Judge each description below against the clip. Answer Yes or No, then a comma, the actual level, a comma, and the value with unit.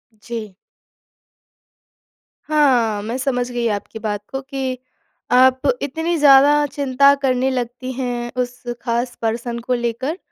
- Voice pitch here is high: Yes, very high, 250 Hz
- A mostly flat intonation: Yes, narrow, 2.3 semitones